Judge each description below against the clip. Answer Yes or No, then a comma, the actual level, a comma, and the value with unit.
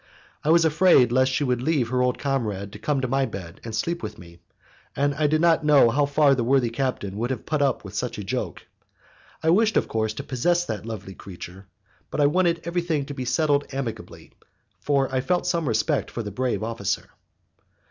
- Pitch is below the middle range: Yes, low, 130 Hz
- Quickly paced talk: Yes, fast, 210 wpm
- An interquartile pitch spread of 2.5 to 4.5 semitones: No, average, 5.1 semitones